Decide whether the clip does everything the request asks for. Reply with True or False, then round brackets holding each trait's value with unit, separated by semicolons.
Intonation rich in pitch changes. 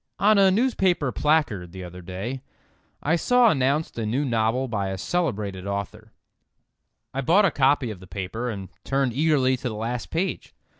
True (7.3 semitones)